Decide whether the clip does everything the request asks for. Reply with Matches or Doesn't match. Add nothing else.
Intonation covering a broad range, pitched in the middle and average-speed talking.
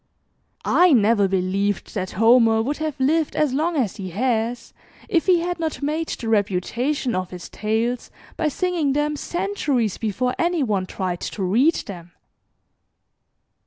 Doesn't match